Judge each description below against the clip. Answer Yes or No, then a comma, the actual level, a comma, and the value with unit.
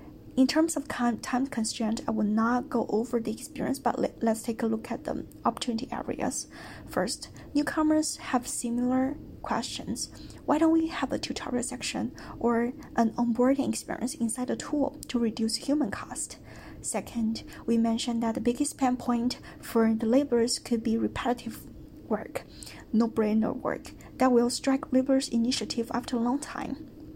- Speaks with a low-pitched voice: No, high, 245 Hz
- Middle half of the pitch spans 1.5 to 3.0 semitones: Yes, average, 2.7 semitones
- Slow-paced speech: No, average, 155 wpm